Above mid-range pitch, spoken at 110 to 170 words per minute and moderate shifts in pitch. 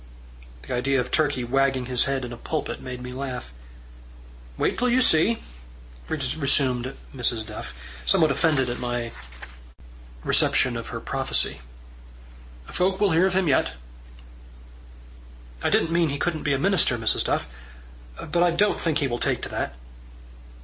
No: low, 135 Hz; average, 155 wpm; average, 5.0 semitones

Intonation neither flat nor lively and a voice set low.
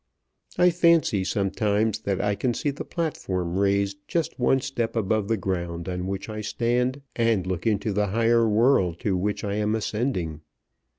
Yes: average, 3.5 semitones; low, 105 Hz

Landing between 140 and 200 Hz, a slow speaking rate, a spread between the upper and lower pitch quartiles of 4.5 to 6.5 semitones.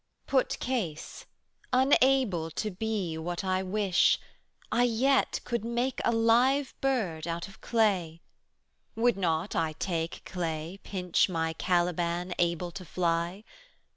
Yes: medium, 185 Hz; slow, 130 wpm; average, 5.3 semitones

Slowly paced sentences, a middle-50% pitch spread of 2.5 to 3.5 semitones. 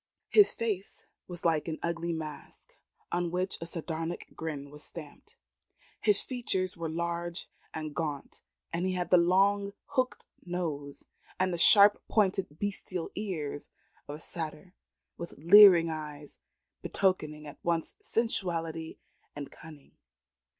Yes: slow, 130 wpm; average, 3.0 semitones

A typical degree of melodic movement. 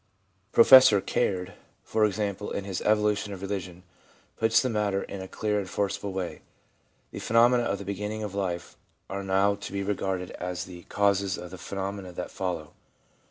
No: narrow, 1.9 semitones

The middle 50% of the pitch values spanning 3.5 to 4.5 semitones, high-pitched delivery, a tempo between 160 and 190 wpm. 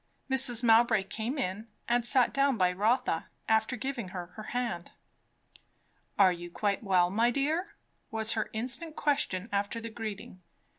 No: average, 4.0 semitones; high, 225 Hz; average, 150 wpm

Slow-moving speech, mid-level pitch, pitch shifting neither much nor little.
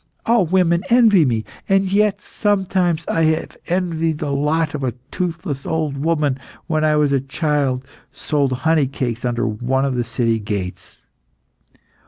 No: average, 160 wpm; medium, 150 Hz; average, 4.7 semitones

